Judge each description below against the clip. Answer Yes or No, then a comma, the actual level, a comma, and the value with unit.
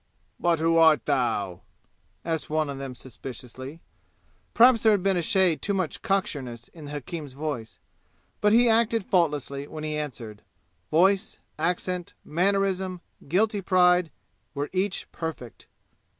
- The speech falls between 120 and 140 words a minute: Yes, slow, 135 wpm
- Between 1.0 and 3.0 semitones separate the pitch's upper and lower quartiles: No, average, 5.2 semitones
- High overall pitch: No, medium, 165 Hz